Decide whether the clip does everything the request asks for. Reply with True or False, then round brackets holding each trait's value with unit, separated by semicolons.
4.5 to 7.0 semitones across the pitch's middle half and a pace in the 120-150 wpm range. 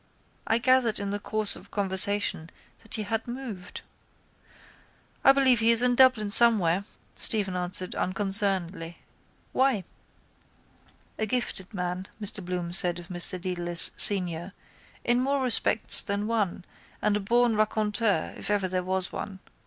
False (3.8 semitones; 140 wpm)